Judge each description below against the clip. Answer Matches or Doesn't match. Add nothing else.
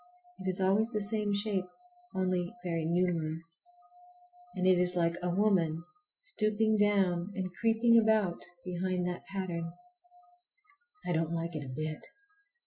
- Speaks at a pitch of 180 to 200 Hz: Matches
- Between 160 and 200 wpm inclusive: Doesn't match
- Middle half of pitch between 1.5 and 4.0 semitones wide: Matches